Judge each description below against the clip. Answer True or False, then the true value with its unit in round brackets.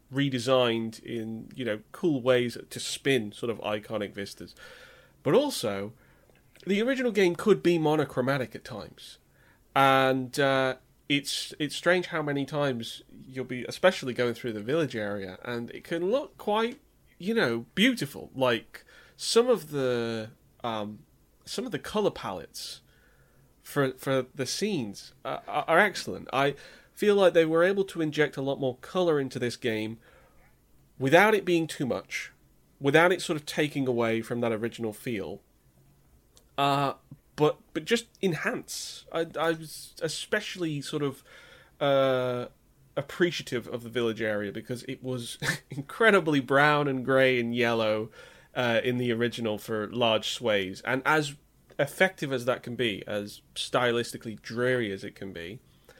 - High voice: False (135 Hz)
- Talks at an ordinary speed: True (150 wpm)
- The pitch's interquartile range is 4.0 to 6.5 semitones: True (4.8 semitones)